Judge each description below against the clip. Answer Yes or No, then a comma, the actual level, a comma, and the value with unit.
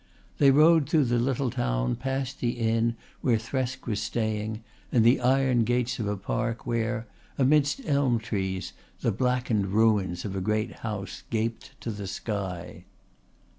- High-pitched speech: No, low, 115 Hz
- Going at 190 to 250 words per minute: No, average, 155 wpm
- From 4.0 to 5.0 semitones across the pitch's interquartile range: No, average, 3.3 semitones